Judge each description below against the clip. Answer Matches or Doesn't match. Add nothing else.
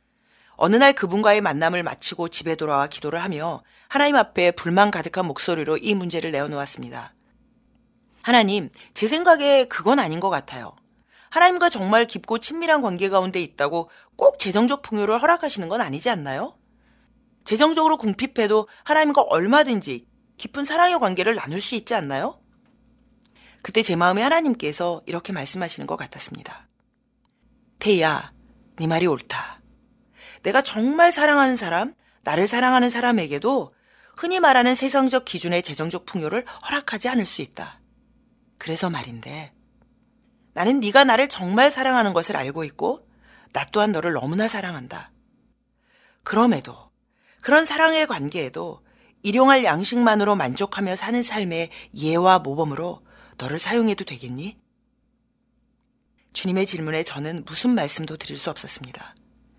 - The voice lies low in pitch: Doesn't match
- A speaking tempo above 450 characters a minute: Doesn't match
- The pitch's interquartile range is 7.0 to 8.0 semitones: Doesn't match